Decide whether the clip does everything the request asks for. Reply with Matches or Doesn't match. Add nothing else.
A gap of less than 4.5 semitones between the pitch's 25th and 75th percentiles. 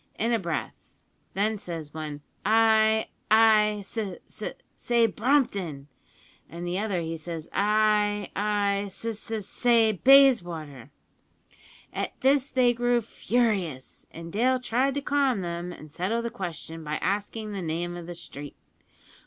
Doesn't match